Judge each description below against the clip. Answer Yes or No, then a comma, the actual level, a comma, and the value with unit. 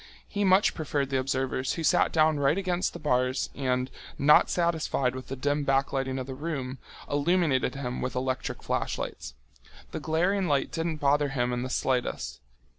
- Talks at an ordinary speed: Yes, average, 170 wpm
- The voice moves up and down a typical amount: Yes, average, 3.6 semitones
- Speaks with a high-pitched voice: No, medium, 140 Hz